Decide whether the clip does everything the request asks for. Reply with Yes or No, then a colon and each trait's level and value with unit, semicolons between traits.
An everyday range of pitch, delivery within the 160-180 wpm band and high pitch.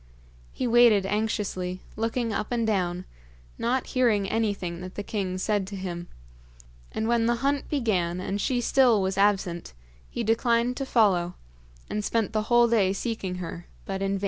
Yes: average, 3.8 semitones; average, 170 wpm; high, 210 Hz